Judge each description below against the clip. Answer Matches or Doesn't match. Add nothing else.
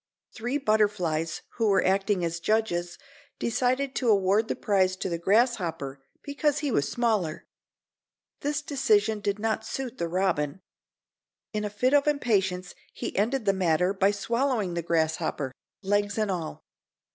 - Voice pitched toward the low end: Doesn't match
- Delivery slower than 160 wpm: Matches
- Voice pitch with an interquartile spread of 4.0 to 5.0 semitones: Matches